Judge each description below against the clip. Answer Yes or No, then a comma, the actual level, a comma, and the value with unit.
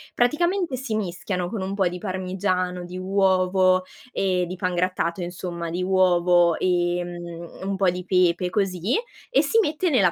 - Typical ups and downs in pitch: No, narrow, 1.8 semitones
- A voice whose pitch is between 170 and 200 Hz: Yes, medium, 185 Hz